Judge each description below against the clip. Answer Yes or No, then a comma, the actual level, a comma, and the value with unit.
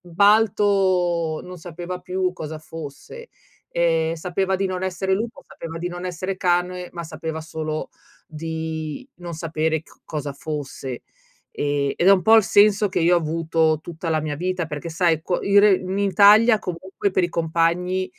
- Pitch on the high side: No, medium, 175 Hz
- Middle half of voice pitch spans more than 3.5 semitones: No, average, 2.8 semitones